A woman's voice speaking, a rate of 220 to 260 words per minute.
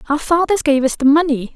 Yes: female; fast, 230 wpm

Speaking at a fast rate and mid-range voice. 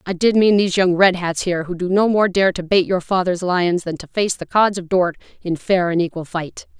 Yes: fast, 265 wpm; medium, 180 Hz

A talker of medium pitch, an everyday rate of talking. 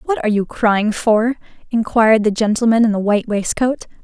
No: high, 220 Hz; average, 180 wpm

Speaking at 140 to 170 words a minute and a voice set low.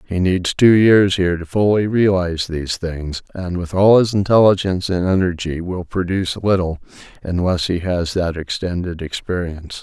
Yes: average, 160 wpm; very low, 90 Hz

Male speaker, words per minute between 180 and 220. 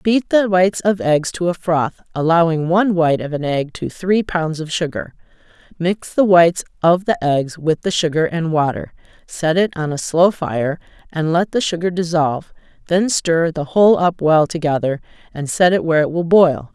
No: female; average, 195 wpm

